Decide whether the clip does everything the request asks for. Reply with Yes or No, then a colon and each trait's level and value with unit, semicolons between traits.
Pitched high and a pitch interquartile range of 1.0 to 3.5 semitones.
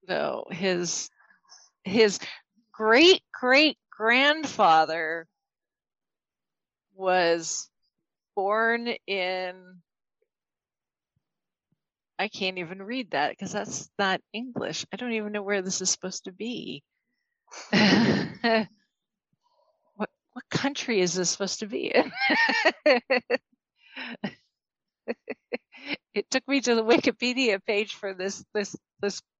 No: high, 215 Hz; average, 4.9 semitones